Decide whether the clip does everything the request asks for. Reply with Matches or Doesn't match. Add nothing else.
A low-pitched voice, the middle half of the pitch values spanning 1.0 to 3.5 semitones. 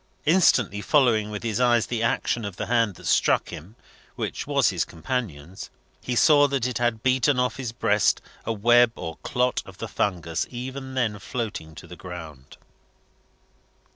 Doesn't match